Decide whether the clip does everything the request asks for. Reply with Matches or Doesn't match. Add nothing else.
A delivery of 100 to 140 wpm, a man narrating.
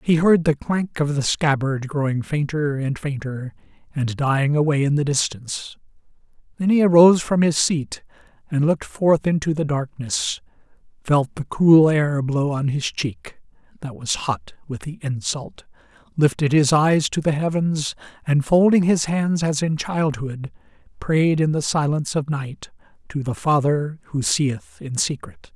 Doesn't match